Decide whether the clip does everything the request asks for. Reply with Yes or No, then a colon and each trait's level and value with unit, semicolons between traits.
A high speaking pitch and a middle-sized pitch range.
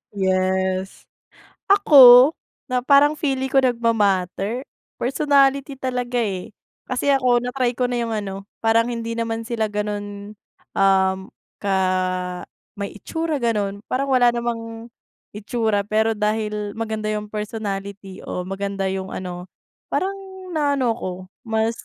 Yes: high, 225 Hz; average, 3.8 semitones